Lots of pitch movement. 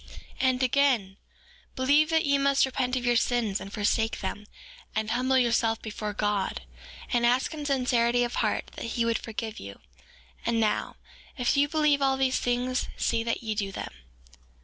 No: average, 3.1 semitones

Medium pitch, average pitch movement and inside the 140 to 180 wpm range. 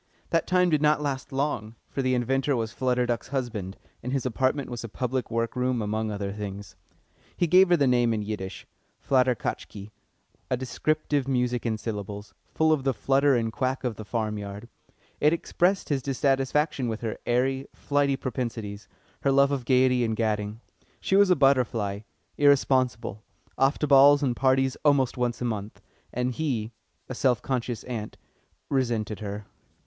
No: low, 125 Hz; average, 3.7 semitones; average, 170 wpm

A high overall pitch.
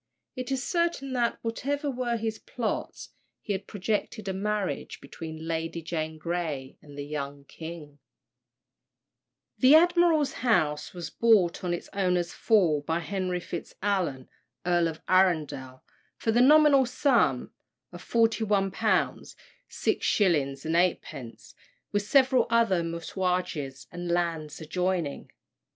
No: medium, 180 Hz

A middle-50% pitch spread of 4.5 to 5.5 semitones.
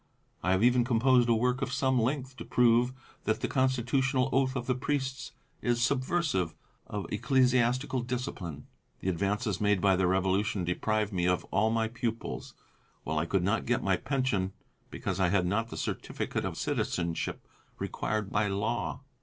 Yes: average, 4.8 semitones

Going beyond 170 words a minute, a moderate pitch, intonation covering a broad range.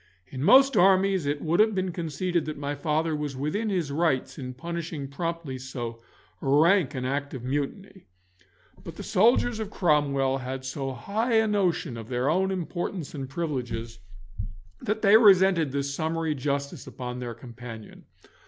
No: average, 160 wpm; medium, 150 Hz; wide, 5.7 semitones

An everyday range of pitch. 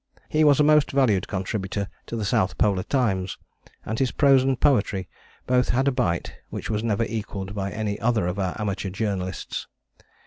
Yes: average, 4.8 semitones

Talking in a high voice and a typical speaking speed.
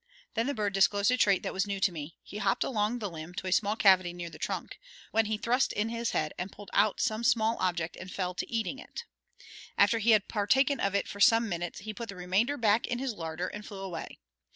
No: high, 205 Hz; fast, 245 wpm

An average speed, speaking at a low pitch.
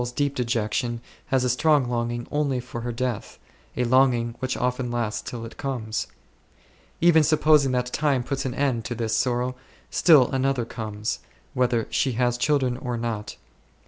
Yes: average, 165 wpm; low, 125 Hz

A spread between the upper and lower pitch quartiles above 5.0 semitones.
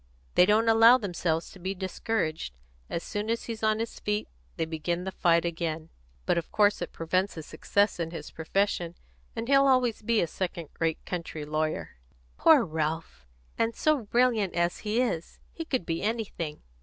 Yes: wide, 5.4 semitones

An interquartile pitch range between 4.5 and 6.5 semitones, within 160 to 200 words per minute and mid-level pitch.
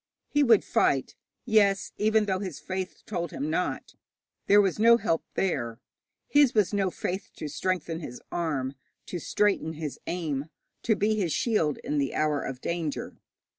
Yes: wide, 5.4 semitones; average, 165 wpm; medium, 180 Hz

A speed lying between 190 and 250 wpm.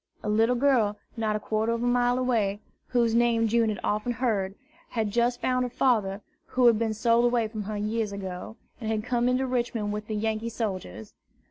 Yes: fast, 205 wpm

